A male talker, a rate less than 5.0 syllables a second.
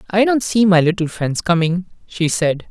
Yes: male; 4.8 syllables/s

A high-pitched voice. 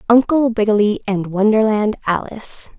Yes: high, 215 Hz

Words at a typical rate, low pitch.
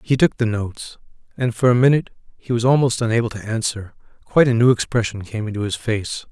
No: fast, 210 wpm; low, 115 Hz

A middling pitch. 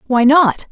No: very high, 270 Hz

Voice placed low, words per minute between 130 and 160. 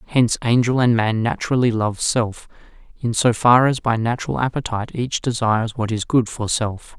No: low, 115 Hz; average, 180 wpm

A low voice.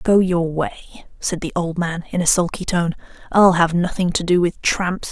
No: medium, 175 Hz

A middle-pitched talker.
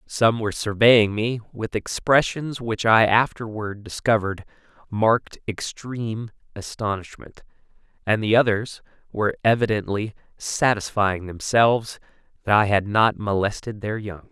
No: low, 110 Hz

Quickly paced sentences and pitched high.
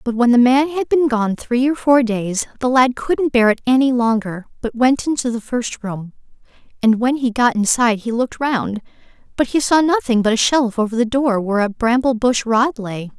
Yes: fast, 220 wpm; high, 240 Hz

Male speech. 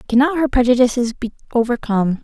No: female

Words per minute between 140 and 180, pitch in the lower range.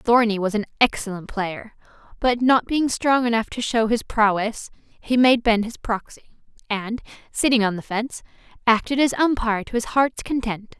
No: average, 170 wpm; high, 230 Hz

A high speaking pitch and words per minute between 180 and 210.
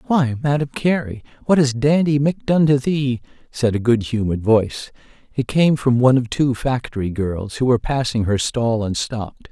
No: low, 125 Hz; average, 190 wpm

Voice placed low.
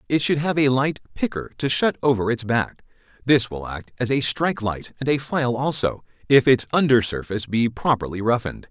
Yes: low, 125 Hz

